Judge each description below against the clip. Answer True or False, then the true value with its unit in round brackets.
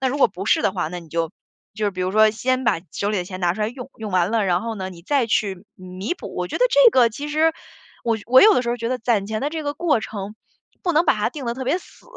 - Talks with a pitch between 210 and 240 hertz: True (220 Hz)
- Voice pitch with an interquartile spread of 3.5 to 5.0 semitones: False (5.5 semitones)